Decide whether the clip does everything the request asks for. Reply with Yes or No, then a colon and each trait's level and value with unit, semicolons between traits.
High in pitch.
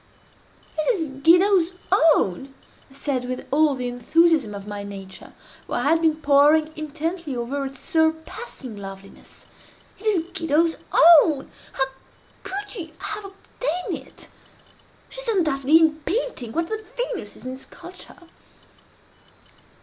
Yes: very high, 310 Hz